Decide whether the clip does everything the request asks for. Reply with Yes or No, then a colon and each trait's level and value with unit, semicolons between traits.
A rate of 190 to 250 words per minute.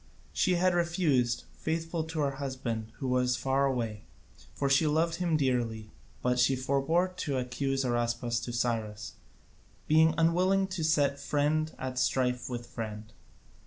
No: average, 145 wpm